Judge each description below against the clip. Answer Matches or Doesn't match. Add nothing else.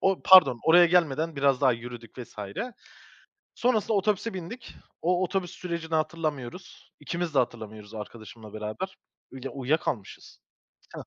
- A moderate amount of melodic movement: Doesn't match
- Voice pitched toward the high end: Doesn't match